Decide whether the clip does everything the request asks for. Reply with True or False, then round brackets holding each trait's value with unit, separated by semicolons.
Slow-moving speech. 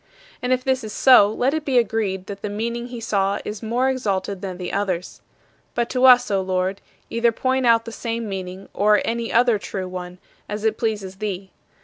False (205 wpm)